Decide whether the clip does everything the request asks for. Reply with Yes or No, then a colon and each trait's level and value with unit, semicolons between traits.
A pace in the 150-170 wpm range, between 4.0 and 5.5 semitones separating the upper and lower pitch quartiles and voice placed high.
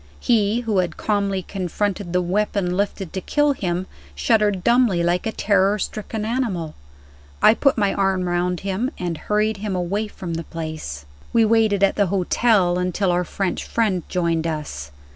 No: average, 165 wpm; average, 3.1 semitones; high, 195 Hz